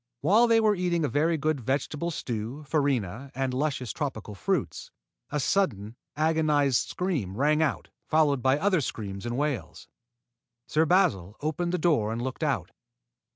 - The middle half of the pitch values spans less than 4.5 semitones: No, average, 5.0 semitones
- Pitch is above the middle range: No, medium, 145 Hz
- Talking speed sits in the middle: Yes, average, 155 wpm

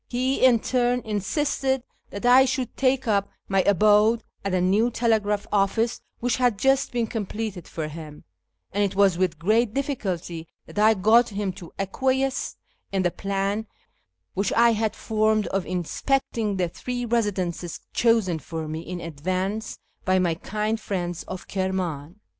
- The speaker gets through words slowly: No, average, 155 wpm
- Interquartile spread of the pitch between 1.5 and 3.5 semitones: No, average, 4.2 semitones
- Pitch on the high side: Yes, high, 205 Hz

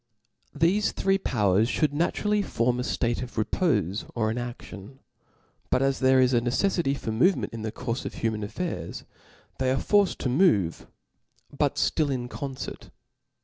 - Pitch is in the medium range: No, low, 130 Hz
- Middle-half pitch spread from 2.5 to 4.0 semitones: No, average, 5.3 semitones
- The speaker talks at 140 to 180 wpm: Yes, average, 150 wpm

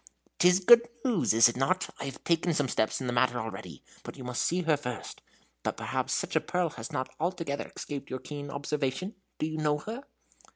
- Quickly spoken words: Yes, fast, 215 wpm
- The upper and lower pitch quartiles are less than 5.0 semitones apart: No, average, 5.3 semitones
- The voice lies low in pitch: No, medium, 150 Hz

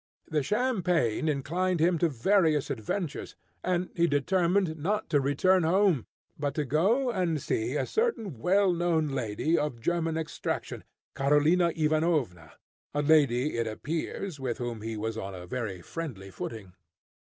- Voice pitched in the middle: Yes, medium, 155 Hz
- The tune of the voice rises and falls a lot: Yes, wide, 5.9 semitones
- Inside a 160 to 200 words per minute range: No, average, 145 wpm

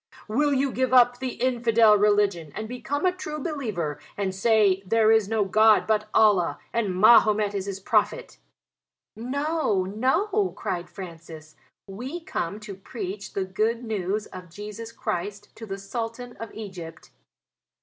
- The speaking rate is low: No, average, 150 wpm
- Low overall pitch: No, high, 215 Hz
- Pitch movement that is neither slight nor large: Yes, average, 4.0 semitones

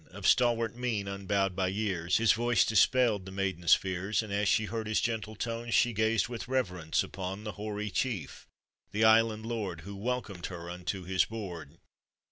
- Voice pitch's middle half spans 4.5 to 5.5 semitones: No, average, 3.3 semitones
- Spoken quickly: No, average, 175 wpm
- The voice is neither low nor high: No, low, 105 Hz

